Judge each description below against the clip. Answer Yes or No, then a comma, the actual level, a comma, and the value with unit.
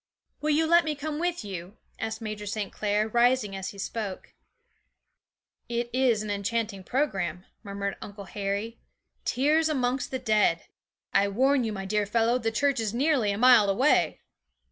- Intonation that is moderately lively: Yes, average, 4.3 semitones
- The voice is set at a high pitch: Yes, high, 225 Hz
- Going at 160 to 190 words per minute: Yes, average, 165 wpm